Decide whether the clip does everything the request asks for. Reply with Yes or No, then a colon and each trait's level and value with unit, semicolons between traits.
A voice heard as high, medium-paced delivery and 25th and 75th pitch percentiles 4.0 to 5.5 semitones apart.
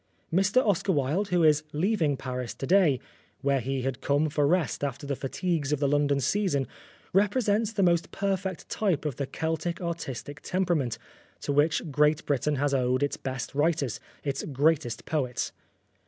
No: medium, 150 Hz; average, 165 wpm; average, 4.5 semitones